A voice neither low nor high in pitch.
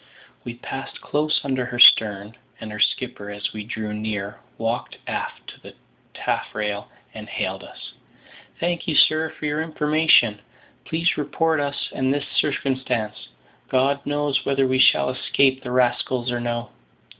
No: low, 130 Hz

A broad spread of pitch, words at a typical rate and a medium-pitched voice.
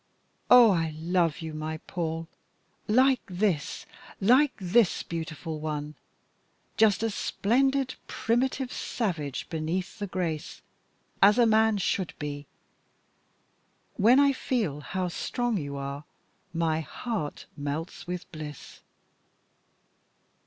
No: wide, 6.4 semitones; slow, 110 wpm; medium, 180 Hz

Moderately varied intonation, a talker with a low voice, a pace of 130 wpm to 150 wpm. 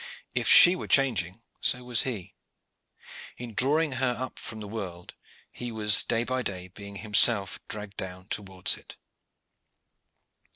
Yes: average, 4.1 semitones; low, 110 Hz; average, 140 wpm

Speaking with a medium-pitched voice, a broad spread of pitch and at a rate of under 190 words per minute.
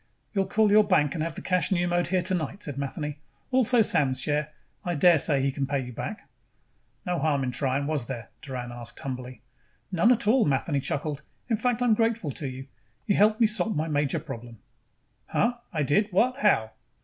No: medium, 155 Hz; wide, 7.0 semitones; average, 195 wpm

